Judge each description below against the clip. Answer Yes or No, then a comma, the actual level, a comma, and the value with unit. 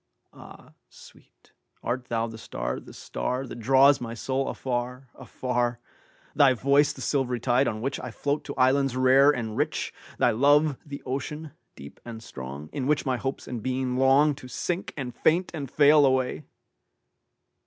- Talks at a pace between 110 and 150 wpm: Yes, average, 145 wpm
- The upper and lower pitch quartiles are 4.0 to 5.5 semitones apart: No, narrow, 2.6 semitones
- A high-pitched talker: No, low, 130 Hz